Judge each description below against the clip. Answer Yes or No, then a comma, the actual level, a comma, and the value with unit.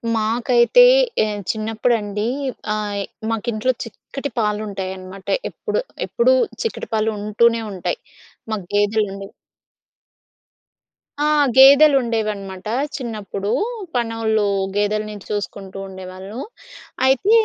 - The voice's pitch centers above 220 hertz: No, high, 215 Hz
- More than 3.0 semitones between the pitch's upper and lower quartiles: No, narrow, 2.5 semitones